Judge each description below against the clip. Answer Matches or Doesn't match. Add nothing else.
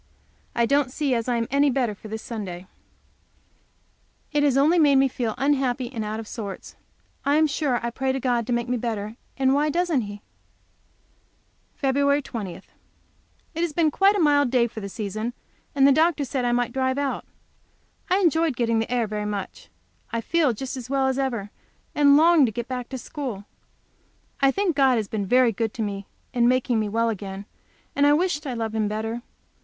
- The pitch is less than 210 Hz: Doesn't match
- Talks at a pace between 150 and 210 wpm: Matches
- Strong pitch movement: Doesn't match